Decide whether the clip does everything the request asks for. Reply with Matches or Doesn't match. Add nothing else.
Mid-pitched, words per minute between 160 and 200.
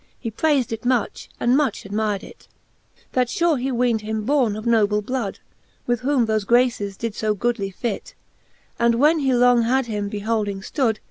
Doesn't match